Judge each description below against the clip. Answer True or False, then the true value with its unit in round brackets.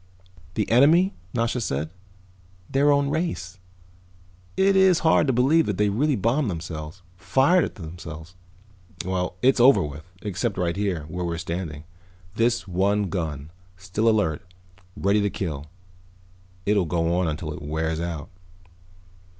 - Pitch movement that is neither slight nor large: False (6.8 semitones)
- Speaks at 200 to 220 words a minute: False (140 wpm)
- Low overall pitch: True (95 Hz)